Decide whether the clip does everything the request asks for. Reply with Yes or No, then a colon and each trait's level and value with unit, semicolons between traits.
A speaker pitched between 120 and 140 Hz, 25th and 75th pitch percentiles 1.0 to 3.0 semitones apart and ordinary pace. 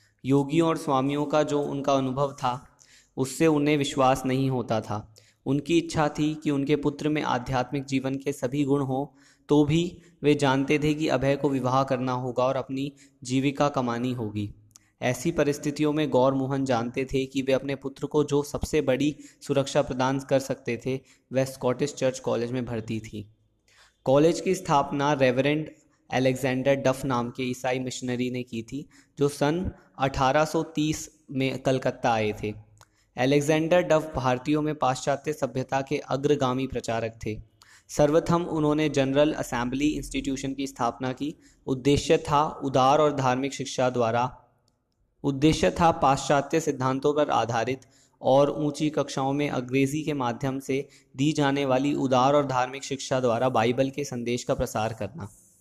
Yes: low, 135 Hz; narrow, 2.4 semitones; average, 155 wpm